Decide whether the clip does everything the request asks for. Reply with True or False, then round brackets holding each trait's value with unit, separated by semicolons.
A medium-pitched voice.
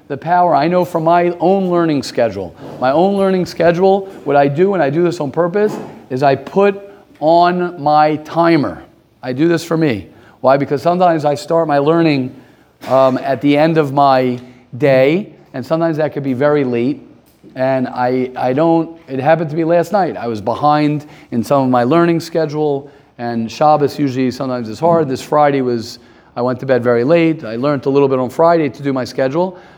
True (150 Hz)